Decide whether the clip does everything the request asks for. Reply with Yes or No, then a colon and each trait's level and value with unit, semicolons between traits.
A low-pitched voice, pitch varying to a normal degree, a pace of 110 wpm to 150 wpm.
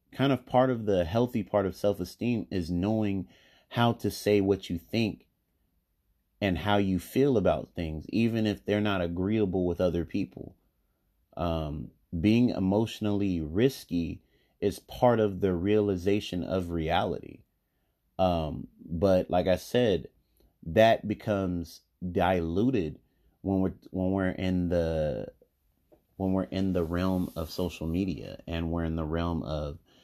Yes: very low, 95 Hz; average, 3.3 semitones; average, 140 wpm